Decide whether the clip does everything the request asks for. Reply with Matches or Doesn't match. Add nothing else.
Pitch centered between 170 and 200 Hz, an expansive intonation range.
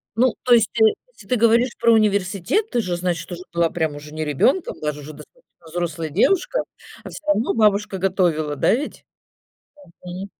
Matches